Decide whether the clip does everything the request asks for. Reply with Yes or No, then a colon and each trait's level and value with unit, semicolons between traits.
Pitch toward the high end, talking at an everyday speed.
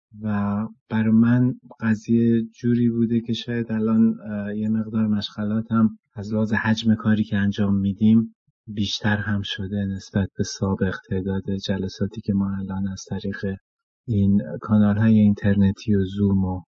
No: low, 105 Hz; average, 145 wpm